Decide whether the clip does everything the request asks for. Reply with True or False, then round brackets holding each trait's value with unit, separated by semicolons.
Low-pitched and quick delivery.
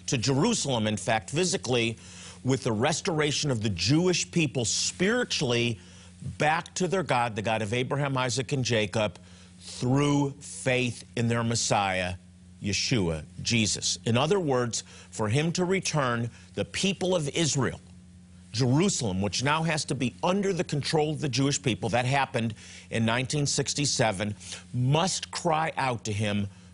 False (125 Hz; 145 wpm)